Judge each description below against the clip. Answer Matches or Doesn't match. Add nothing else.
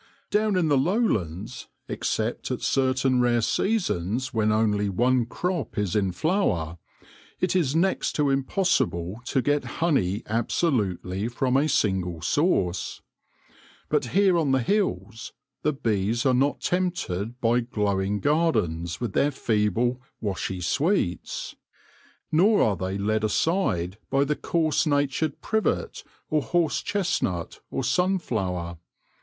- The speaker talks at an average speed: Doesn't match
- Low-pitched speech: Matches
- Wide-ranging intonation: Matches